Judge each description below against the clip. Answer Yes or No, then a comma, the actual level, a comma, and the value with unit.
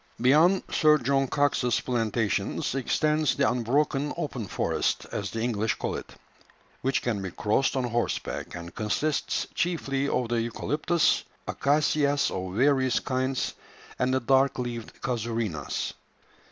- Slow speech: Yes, slow, 130 wpm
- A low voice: Yes, low, 130 Hz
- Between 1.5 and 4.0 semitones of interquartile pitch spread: Yes, average, 3.7 semitones